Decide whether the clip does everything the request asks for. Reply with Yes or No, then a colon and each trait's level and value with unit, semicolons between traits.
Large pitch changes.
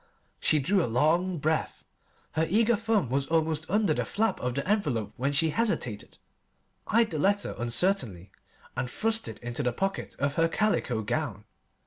Yes: wide, 8.2 semitones